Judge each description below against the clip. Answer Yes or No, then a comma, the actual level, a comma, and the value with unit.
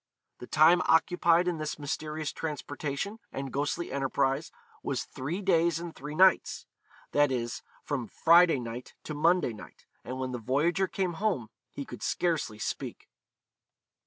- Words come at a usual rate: Yes, average, 145 wpm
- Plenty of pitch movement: No, average, 4.2 semitones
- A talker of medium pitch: Yes, medium, 155 Hz